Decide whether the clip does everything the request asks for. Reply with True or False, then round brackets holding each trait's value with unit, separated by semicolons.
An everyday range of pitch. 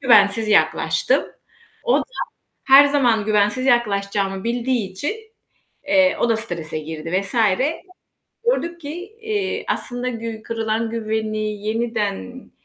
True (4.1 semitones)